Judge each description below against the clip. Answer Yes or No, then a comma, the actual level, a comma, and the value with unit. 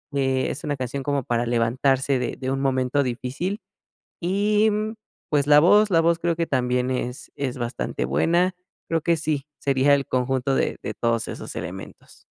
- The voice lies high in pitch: No, low, 135 Hz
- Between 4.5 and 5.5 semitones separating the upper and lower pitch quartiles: Yes, average, 4.8 semitones